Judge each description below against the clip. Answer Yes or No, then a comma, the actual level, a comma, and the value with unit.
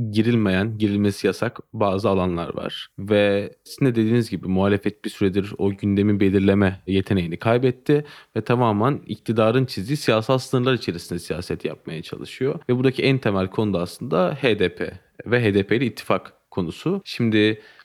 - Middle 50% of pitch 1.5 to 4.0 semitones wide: Yes, average, 3.6 semitones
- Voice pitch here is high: No, low, 105 Hz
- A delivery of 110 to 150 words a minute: Yes, fast, 140 wpm